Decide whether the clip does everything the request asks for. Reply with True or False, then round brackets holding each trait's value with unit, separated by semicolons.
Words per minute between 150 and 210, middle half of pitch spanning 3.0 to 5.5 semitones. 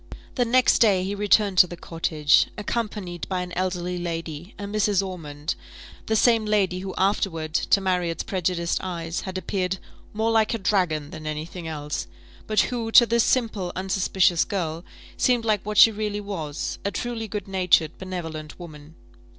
True (165 wpm; 3.8 semitones)